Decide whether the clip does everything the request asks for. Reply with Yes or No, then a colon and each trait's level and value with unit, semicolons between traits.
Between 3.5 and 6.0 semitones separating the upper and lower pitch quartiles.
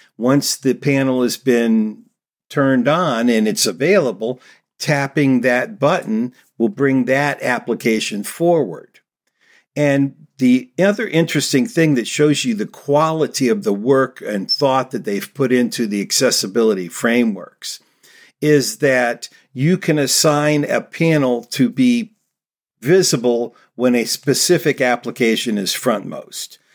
Yes: average, 4.9 semitones